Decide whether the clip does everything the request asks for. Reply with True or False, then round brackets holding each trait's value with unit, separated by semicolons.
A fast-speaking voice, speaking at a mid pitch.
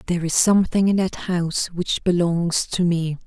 False (185 wpm; 175 Hz)